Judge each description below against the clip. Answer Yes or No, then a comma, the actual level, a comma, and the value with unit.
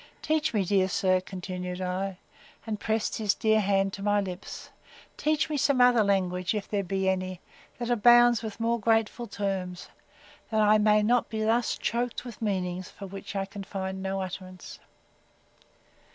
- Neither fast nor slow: Yes, average, 165 wpm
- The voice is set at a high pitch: Yes, high, 200 Hz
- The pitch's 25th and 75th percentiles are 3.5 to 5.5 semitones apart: No, average, 3.0 semitones